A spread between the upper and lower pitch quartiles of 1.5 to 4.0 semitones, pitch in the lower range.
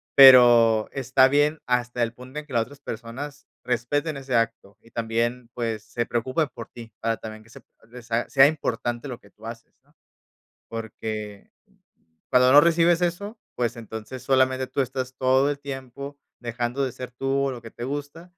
Yes: average, 3.0 semitones; low, 125 Hz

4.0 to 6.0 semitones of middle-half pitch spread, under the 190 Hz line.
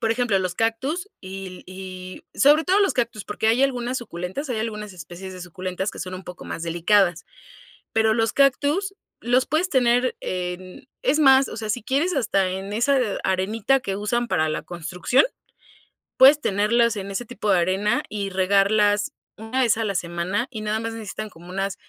No: average, 4.7 semitones; high, 210 Hz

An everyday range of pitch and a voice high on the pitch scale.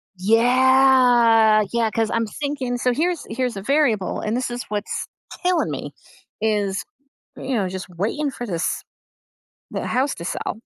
Yes: average, 3.7 semitones; high, 235 Hz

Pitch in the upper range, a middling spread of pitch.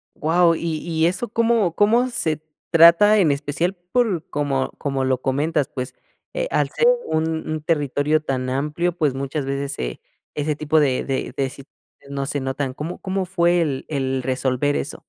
No: medium, 150 Hz; average, 3.9 semitones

